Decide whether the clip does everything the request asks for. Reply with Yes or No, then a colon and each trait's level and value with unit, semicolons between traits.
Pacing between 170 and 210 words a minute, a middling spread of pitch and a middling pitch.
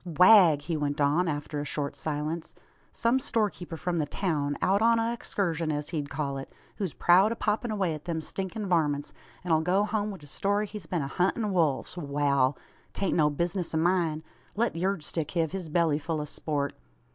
Yes: average, 200 wpm; average, 4.6 semitones; medium, 165 Hz